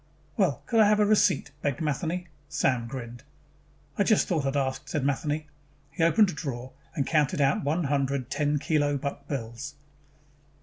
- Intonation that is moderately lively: Yes, average, 3.2 semitones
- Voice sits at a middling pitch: Yes, medium, 145 Hz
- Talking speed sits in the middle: Yes, average, 170 wpm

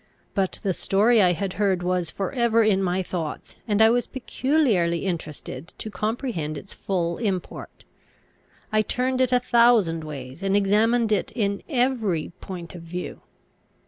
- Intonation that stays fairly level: No, average, 4.7 semitones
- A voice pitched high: Yes, high, 200 Hz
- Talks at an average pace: Yes, average, 155 wpm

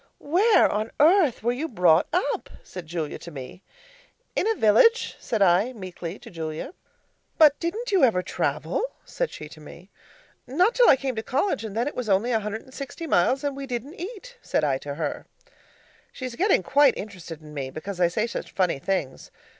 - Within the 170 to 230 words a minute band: Yes, average, 195 wpm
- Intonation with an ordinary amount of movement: No, wide, 8.8 semitones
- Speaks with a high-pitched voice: Yes, high, 225 Hz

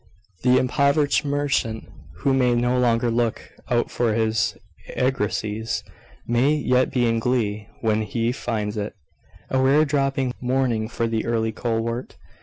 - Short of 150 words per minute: Yes, average, 140 wpm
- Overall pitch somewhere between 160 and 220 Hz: No, low, 120 Hz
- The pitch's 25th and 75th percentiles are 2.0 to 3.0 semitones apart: Yes, average, 2.7 semitones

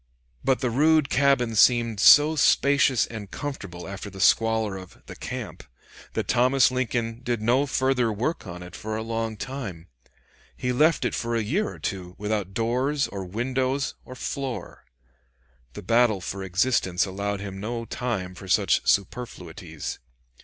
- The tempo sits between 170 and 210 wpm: No, average, 155 wpm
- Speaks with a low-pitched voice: Yes, low, 115 Hz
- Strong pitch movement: No, average, 4.5 semitones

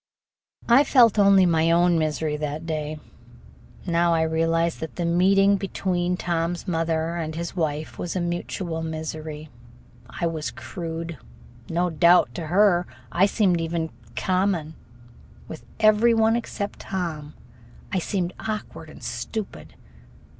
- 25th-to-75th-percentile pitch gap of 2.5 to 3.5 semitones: Yes, average, 2.8 semitones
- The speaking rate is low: Yes, slow, 130 wpm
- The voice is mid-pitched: Yes, medium, 170 Hz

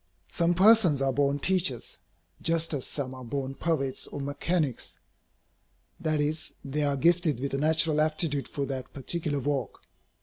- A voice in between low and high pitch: Yes, medium, 145 Hz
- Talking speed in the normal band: Yes, average, 155 wpm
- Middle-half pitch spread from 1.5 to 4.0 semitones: Yes, average, 3.1 semitones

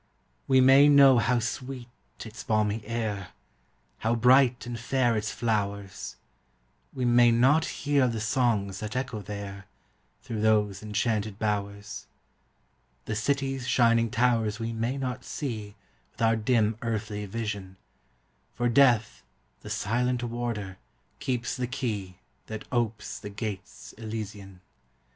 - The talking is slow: Yes, slow, 125 wpm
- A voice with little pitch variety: No, average, 3.0 semitones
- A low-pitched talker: Yes, low, 115 Hz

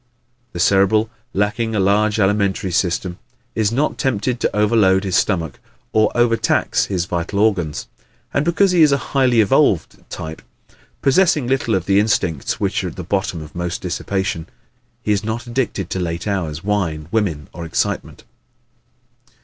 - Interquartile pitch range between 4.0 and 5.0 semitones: Yes, average, 4.3 semitones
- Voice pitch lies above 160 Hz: No, low, 100 Hz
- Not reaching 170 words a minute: Yes, average, 155 wpm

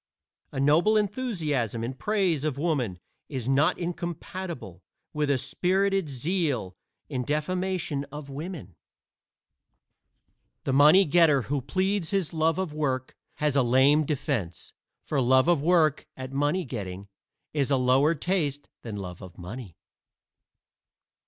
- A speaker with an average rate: No, slow, 130 wpm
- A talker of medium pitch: Yes, medium, 145 Hz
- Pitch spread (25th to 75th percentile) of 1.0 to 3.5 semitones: No, average, 4.8 semitones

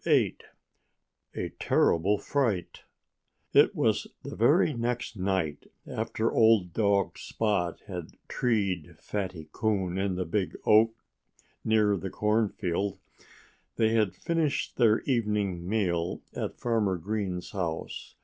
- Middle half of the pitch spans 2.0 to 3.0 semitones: No, average, 3.5 semitones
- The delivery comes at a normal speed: No, slow, 115 wpm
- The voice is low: Yes, low, 100 Hz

